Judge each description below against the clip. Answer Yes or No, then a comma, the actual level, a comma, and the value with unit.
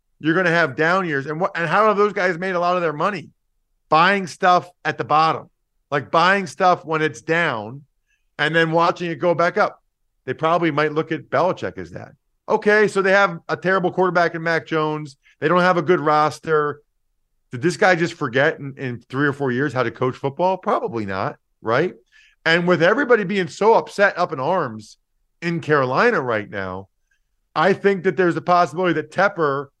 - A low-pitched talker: No, medium, 165 Hz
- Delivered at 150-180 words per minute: No, average, 200 wpm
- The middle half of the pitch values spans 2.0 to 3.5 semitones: No, average, 3.9 semitones